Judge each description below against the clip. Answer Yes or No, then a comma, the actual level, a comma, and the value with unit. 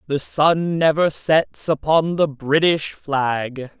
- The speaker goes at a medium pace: No, slow, 125 wpm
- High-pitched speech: No, medium, 140 Hz